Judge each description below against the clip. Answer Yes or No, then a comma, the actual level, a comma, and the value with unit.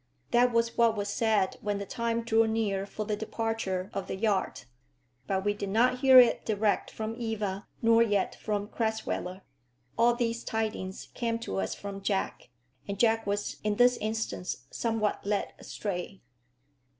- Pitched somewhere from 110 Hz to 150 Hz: No, high, 220 Hz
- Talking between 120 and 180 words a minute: Yes, average, 160 wpm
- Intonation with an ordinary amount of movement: No, narrow, 2.3 semitones